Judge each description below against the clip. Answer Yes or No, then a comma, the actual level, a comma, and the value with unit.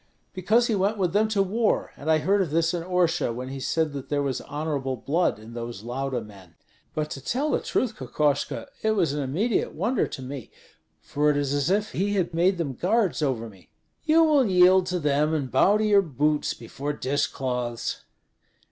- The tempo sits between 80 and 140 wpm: No, fast, 205 wpm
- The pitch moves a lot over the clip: Yes, wide, 6.4 semitones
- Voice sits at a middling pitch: Yes, medium, 155 Hz